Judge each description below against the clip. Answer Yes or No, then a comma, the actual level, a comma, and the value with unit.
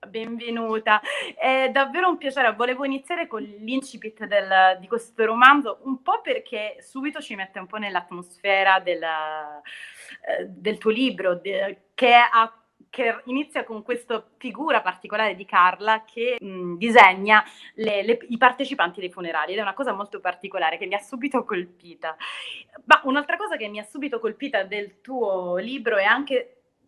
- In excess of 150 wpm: Yes, average, 160 wpm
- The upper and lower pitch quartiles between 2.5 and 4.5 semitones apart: No, average, 5.2 semitones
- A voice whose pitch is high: Yes, high, 225 Hz